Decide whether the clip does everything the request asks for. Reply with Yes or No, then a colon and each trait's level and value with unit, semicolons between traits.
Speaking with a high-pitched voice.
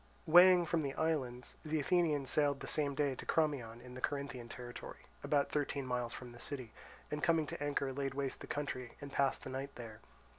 No: medium, 140 Hz